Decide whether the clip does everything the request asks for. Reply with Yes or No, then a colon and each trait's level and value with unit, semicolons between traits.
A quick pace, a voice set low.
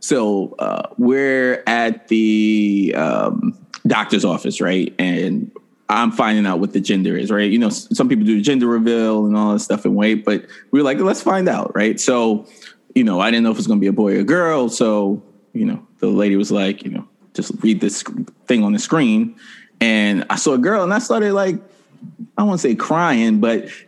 Yes: fast, 225 wpm; low, 120 Hz